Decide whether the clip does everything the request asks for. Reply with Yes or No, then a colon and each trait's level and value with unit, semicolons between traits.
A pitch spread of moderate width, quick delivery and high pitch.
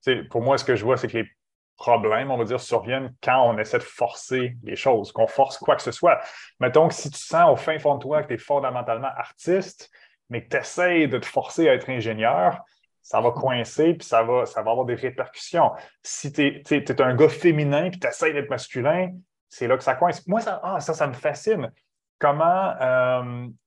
No: average, 3.7 semitones; fast, 230 wpm; low, 135 Hz